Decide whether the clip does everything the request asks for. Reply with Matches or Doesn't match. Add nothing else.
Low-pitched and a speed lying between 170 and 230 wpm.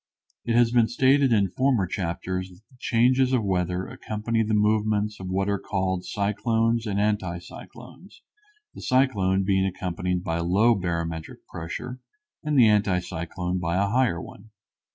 Doesn't match